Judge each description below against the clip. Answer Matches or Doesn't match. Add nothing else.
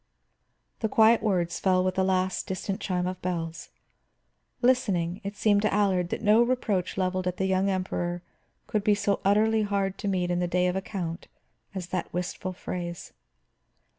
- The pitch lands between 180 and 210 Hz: Matches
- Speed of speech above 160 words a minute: Matches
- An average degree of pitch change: Doesn't match